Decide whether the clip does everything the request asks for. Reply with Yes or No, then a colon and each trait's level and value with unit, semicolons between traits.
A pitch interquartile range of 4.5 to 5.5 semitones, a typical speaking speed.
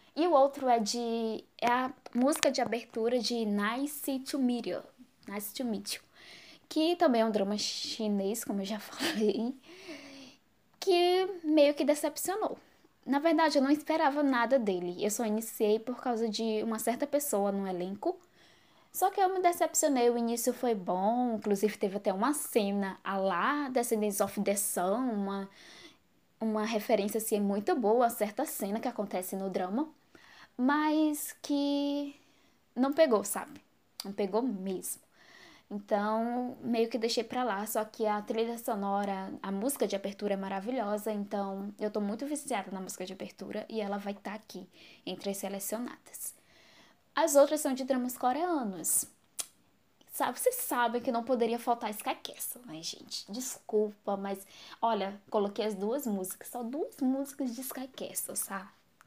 Yes: average, 5.0 semitones; average, 160 wpm